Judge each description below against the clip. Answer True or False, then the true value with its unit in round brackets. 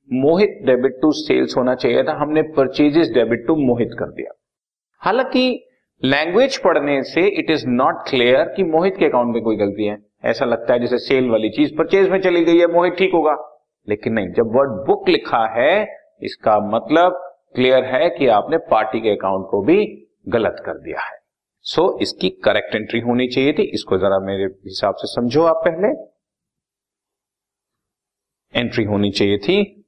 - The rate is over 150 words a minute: True (175 wpm)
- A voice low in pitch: False (145 Hz)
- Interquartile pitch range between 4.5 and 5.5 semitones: False (7.4 semitones)